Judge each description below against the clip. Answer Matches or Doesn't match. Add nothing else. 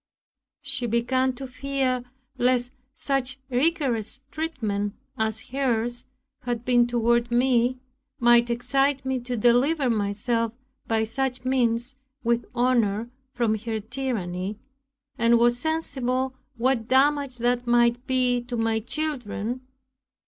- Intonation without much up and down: Matches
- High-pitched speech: Matches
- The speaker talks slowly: Matches